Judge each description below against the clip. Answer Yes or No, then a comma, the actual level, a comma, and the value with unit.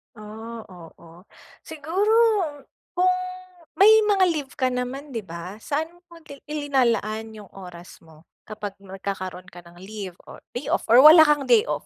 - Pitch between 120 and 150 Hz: No, high, 225 Hz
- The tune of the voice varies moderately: No, wide, 8.0 semitones